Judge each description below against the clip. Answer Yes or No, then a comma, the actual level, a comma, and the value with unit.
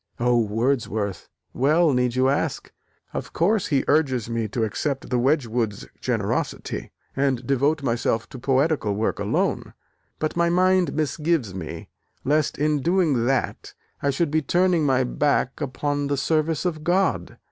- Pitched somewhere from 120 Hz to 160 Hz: Yes, medium, 140 Hz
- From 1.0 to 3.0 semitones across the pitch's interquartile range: No, average, 4.4 semitones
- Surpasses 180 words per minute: No, average, 145 wpm